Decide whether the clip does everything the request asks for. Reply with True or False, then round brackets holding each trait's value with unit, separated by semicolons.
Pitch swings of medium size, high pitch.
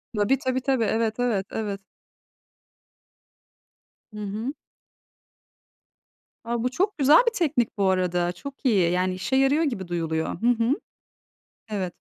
False (5.8 semitones; 225 Hz)